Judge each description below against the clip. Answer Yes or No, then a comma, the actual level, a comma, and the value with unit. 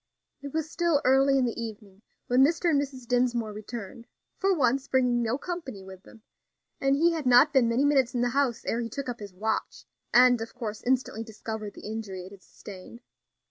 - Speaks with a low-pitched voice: No, high, 245 Hz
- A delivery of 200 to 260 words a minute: Yes, fast, 205 wpm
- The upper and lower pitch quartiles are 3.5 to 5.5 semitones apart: Yes, average, 3.8 semitones